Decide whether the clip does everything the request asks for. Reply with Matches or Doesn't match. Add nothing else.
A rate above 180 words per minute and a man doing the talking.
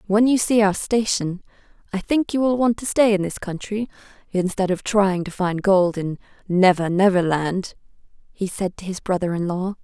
Doesn't match